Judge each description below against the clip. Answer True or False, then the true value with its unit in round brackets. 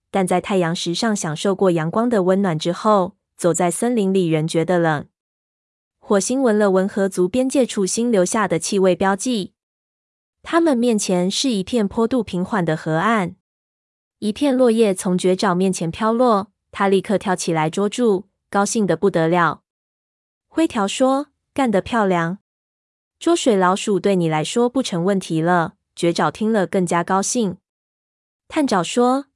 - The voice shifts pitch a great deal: False (4.6 semitones)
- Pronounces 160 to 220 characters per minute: False (230 characters per minute)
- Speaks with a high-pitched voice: True (195 Hz)